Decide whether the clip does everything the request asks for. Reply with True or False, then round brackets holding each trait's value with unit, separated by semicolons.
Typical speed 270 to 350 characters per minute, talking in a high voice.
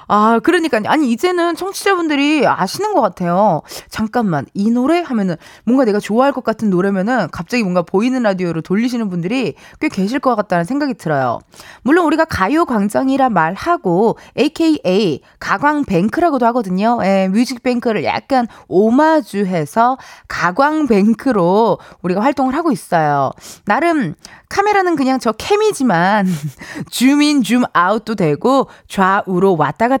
True (330 characters per minute; 230 Hz)